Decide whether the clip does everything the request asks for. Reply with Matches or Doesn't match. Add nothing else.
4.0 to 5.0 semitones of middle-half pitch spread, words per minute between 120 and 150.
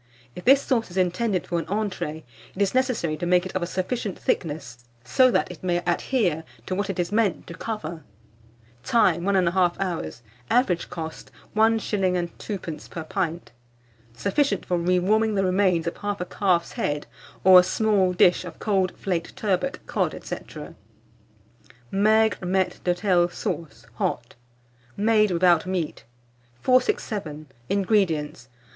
Doesn't match